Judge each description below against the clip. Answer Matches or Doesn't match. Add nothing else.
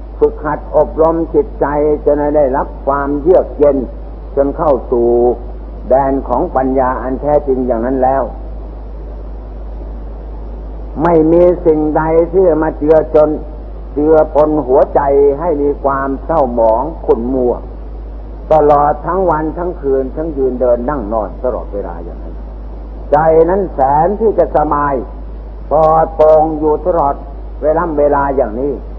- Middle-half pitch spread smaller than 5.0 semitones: Matches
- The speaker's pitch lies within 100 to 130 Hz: Doesn't match